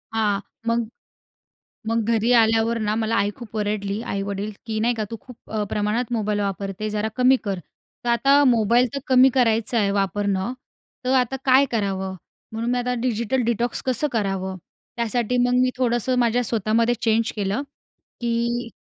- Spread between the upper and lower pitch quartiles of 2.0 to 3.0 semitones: Yes, average, 2.7 semitones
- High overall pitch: Yes, high, 230 Hz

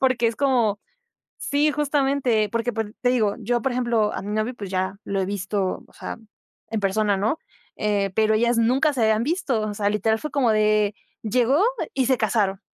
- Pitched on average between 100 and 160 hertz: No, high, 220 Hz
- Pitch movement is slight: No, average, 3.5 semitones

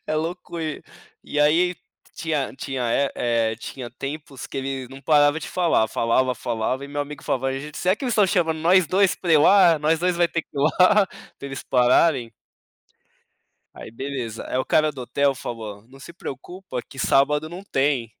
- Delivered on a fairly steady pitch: No, average, 4.4 semitones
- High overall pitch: No, medium, 145 Hz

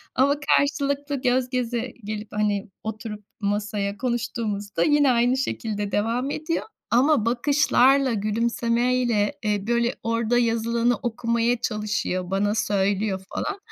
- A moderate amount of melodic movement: Yes, average, 3.1 semitones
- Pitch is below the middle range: No, high, 230 Hz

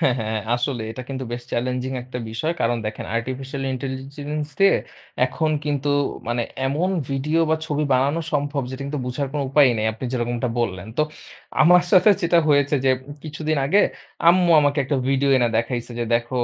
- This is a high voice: No, low, 135 Hz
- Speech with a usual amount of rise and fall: Yes, average, 3.4 semitones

